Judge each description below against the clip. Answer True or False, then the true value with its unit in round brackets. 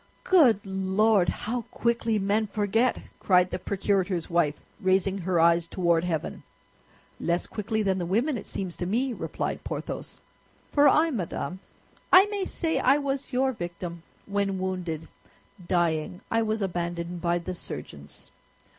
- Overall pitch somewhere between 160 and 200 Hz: True (190 Hz)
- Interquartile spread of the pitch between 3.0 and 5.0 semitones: True (4.5 semitones)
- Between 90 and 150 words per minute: True (145 wpm)